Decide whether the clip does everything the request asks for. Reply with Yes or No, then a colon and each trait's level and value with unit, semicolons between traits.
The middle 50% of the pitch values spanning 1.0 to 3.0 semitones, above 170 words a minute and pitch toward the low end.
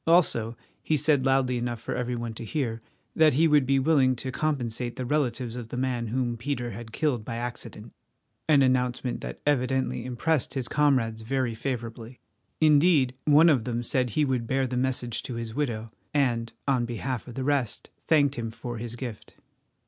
Yes: average, 2.7 semitones; average, 180 wpm; low, 125 Hz